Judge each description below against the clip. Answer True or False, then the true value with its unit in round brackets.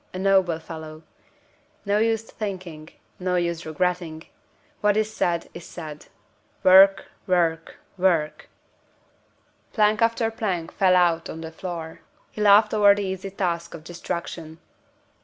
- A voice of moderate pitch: True (180 Hz)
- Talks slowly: True (130 wpm)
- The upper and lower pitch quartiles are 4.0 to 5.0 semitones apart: False (3.5 semitones)